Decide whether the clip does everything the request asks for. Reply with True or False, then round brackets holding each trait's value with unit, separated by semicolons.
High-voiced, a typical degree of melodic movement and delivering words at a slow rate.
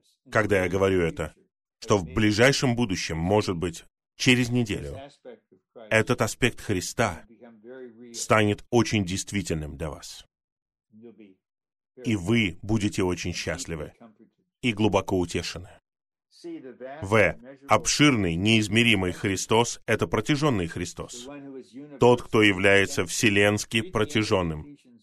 False (110 Hz; 4.3 semitones; 95 wpm)